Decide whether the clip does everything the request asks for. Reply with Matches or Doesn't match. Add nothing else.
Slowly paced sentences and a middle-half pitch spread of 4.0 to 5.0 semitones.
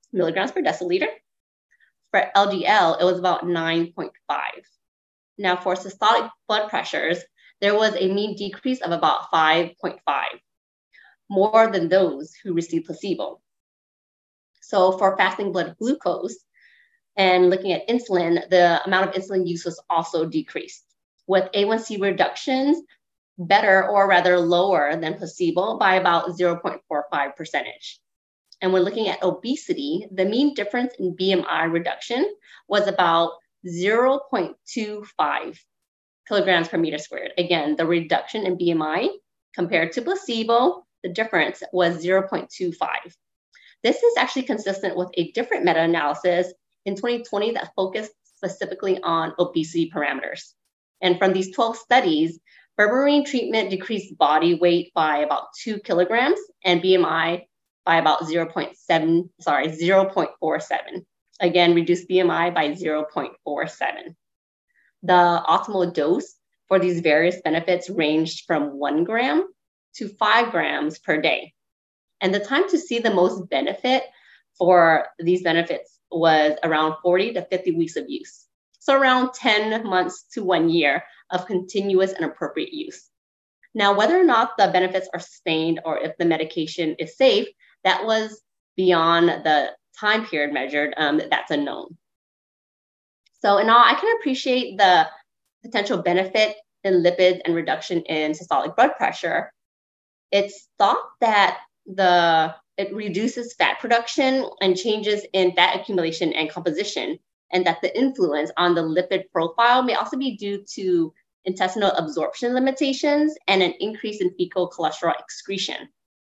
Matches